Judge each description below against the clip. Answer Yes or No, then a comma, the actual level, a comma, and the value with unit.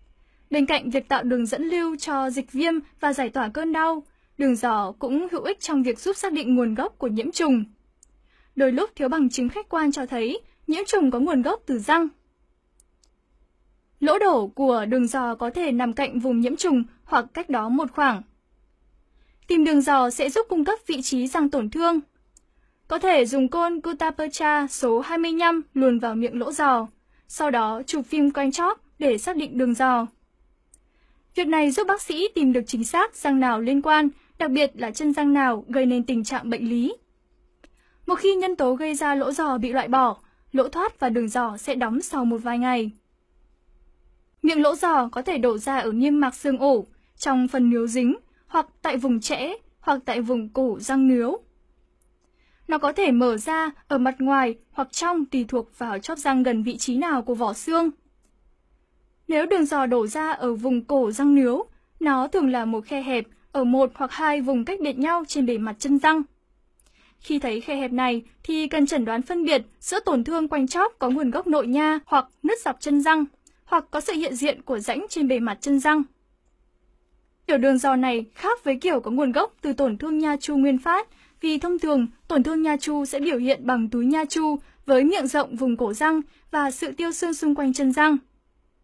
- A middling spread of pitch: Yes, average, 3.9 semitones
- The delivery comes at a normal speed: Yes, average, 205 wpm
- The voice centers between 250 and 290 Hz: Yes, very high, 275 Hz